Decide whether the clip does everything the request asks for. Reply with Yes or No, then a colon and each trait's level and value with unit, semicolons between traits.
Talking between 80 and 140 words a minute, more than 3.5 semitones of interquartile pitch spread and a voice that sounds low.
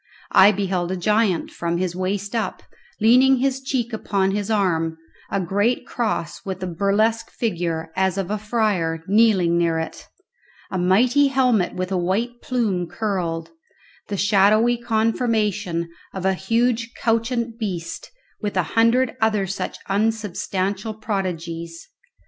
No: slow, 135 wpm; average, 3.9 semitones; high, 200 Hz